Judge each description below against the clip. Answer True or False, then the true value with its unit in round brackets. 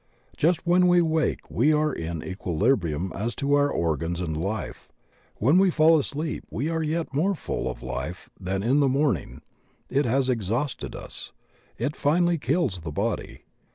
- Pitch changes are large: True (9.0 semitones)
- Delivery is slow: False (170 wpm)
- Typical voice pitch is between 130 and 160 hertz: True (135 Hz)